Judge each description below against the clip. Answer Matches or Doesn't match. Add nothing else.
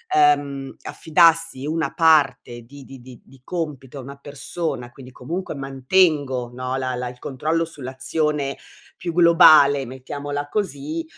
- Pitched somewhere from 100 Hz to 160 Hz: Matches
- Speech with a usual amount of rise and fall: Matches